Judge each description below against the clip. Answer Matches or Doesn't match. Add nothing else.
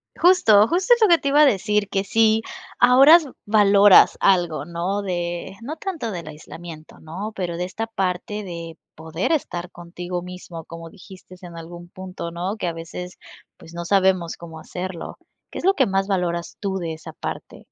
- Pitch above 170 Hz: Matches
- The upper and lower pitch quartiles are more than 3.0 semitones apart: Matches